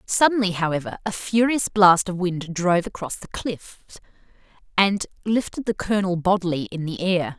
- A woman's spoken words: Yes, female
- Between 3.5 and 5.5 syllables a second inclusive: Yes, 5.1 syllables/s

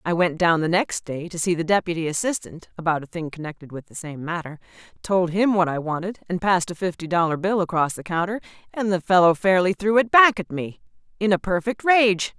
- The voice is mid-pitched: Yes, medium, 180 Hz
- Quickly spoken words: Yes, fast, 225 wpm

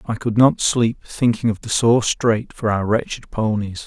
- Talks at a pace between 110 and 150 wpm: No, average, 200 wpm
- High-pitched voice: No, low, 110 Hz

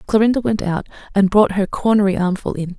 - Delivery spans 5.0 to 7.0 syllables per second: Yes, 5.9 syllables/s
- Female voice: Yes, female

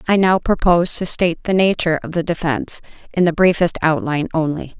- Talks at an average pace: Yes, average, 190 wpm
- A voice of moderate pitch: Yes, medium, 170 Hz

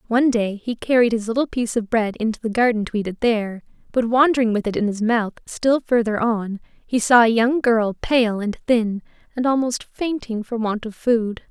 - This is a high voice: Yes, high, 230 Hz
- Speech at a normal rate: No, fast, 215 wpm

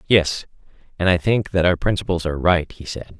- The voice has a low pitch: Yes, very low, 85 Hz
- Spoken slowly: No, fast, 205 wpm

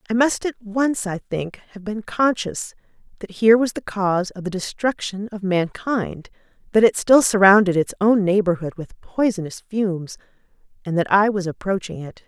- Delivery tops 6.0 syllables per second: No, 4.9 syllables/s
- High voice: Yes, high, 200 Hz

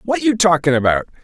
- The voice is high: No, medium, 170 Hz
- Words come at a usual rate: Yes, average, 195 wpm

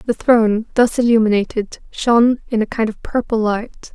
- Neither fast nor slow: Yes, average, 165 wpm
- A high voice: Yes, high, 225 Hz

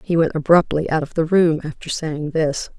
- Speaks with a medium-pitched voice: Yes, medium, 160 Hz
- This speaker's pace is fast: Yes, fast, 215 wpm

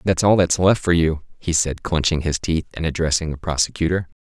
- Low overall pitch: Yes, very low, 85 Hz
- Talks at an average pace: No, fast, 215 wpm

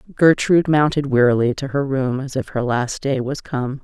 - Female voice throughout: Yes, female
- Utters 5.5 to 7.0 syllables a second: No, 5.1 syllables/s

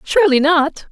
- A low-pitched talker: No, very high, 315 Hz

